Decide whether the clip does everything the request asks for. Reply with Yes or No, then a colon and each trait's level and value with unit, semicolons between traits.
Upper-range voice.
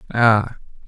No: low, 110 Hz